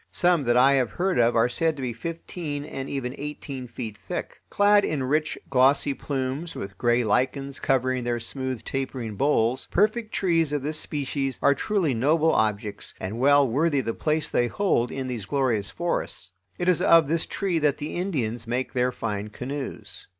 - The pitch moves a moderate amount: Yes, average, 4.3 semitones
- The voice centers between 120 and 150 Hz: Yes, low, 135 Hz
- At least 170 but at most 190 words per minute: Yes, average, 180 wpm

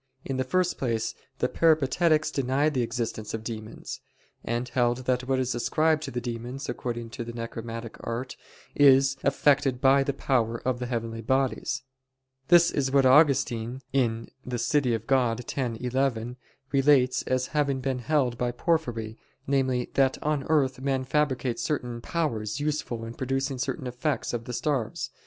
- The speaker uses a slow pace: No, average, 155 wpm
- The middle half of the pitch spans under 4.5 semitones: Yes, average, 2.7 semitones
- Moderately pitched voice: No, low, 130 Hz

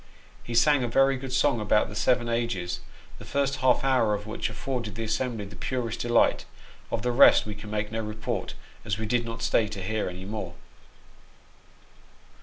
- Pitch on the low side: Yes, low, 115 Hz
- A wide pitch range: No, average, 2.8 semitones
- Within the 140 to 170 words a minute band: No, average, 190 wpm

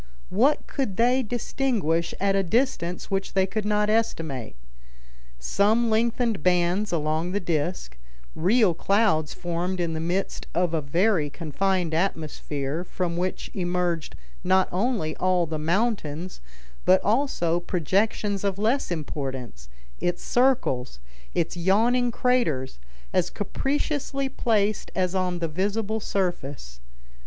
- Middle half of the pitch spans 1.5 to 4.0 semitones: No, average, 4.9 semitones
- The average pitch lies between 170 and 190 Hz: Yes, medium, 185 Hz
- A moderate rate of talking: No, slow, 125 wpm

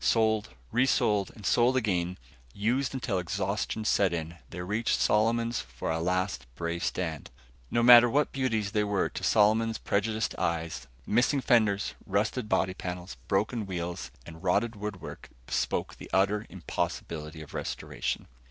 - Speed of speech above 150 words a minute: No, average, 145 wpm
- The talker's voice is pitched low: Yes, low, 105 Hz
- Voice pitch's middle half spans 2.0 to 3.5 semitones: No, average, 4.1 semitones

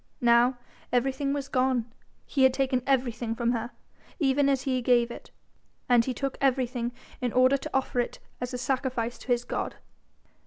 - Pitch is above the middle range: Yes, very high, 255 Hz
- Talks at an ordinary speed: Yes, average, 170 wpm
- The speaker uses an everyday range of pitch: No, narrow, 1.8 semitones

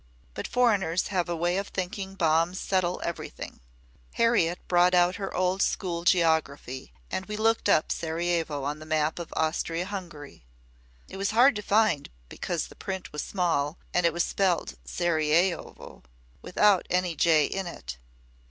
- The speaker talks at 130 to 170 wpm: Yes, average, 155 wpm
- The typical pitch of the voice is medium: Yes, medium, 175 Hz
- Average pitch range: Yes, average, 3.0 semitones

